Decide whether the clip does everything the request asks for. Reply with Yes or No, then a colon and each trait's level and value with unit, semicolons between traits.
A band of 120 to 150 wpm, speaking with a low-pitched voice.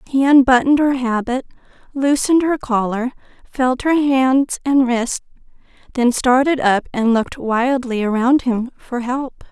No: average, 140 wpm; very high, 255 Hz